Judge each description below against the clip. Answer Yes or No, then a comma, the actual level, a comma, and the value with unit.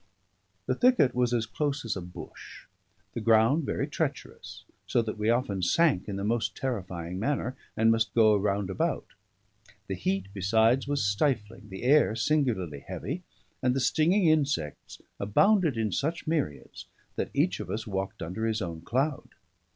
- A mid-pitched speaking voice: No, low, 115 Hz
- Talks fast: No, average, 160 wpm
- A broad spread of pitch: Yes, wide, 5.9 semitones